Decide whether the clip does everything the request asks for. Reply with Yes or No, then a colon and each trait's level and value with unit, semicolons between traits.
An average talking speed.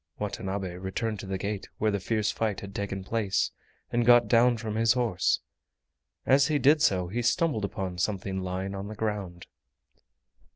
Yes: average, 170 wpm